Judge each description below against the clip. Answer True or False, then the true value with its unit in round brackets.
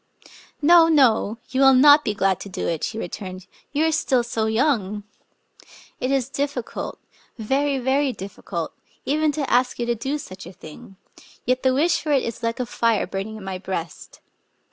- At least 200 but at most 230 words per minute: True (205 wpm)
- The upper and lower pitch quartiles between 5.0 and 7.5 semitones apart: True (5.6 semitones)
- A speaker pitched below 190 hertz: False (245 Hz)